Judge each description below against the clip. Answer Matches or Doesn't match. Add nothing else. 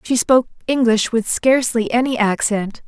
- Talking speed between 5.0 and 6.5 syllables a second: Matches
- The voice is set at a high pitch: Matches